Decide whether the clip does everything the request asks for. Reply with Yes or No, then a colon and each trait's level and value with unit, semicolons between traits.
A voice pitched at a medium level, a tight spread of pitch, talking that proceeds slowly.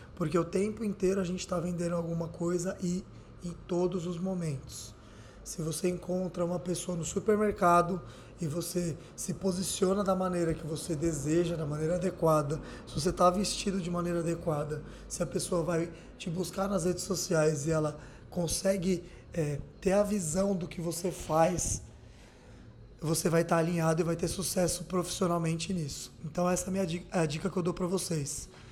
No: medium, 175 Hz; narrow, 2.2 semitones; average, 175 wpm